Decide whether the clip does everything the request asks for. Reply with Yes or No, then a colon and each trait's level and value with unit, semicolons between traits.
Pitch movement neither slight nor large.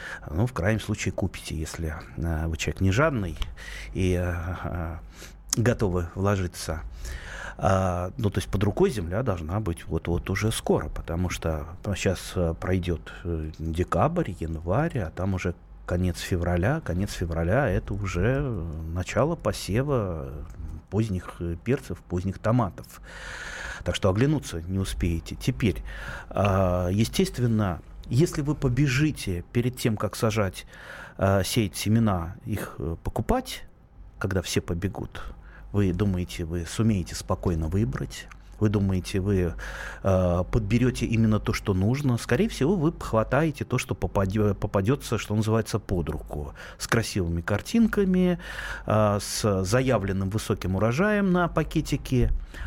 Yes: average, 4.6 semitones